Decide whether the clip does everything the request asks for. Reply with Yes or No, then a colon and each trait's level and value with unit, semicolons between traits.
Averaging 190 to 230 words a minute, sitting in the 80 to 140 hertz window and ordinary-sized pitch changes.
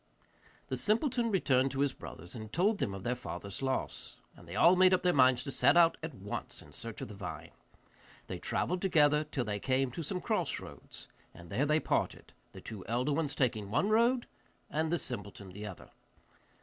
No: average, 200 wpm; low, 135 Hz; wide, 8.3 semitones